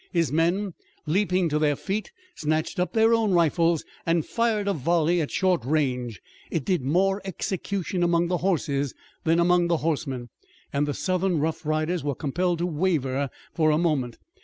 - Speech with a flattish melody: No, average, 3.5 semitones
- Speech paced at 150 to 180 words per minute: Yes, average, 170 wpm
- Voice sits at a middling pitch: Yes, medium, 170 Hz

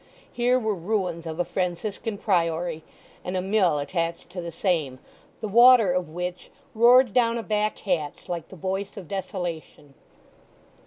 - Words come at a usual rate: Yes, average, 155 wpm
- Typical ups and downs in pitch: Yes, average, 4.1 semitones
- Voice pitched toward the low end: No, medium, 185 Hz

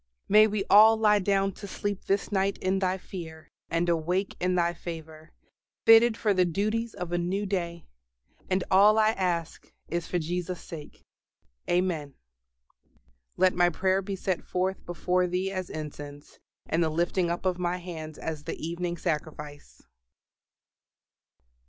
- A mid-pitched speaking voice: Yes, medium, 180 Hz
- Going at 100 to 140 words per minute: No, average, 150 wpm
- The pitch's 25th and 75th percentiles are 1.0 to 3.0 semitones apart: Yes, narrow, 2.6 semitones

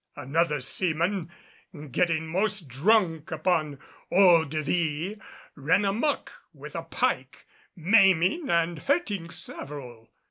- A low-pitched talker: No, medium, 170 Hz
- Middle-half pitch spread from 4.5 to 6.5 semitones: No, average, 4.1 semitones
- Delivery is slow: Yes, slow, 105 wpm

